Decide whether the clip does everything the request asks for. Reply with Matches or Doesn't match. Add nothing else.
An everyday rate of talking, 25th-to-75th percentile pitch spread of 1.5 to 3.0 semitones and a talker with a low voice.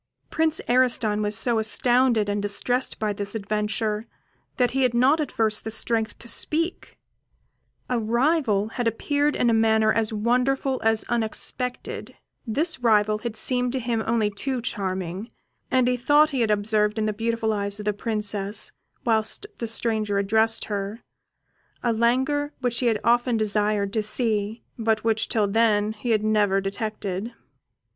Doesn't match